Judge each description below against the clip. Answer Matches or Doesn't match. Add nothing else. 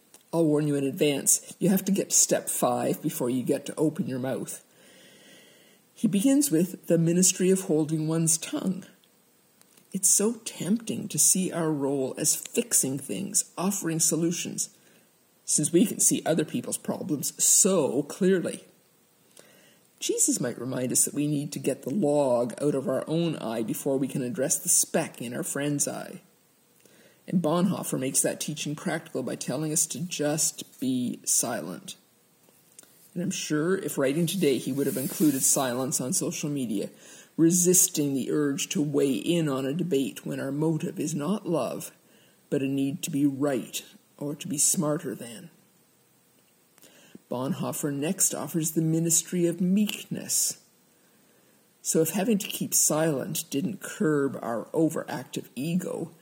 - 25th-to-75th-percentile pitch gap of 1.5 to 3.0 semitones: Doesn't match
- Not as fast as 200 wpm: Matches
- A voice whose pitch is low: Doesn't match